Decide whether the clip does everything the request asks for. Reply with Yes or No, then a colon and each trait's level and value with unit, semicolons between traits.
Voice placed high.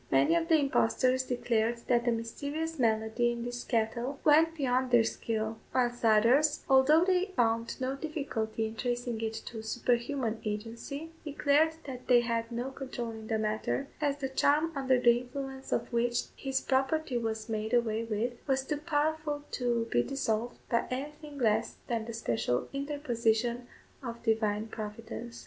Yes: high, 245 Hz